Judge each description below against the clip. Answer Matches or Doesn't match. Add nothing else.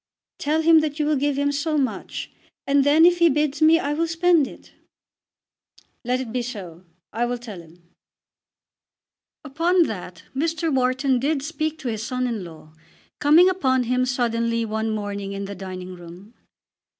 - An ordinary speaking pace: Matches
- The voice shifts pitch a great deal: Matches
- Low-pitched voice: Doesn't match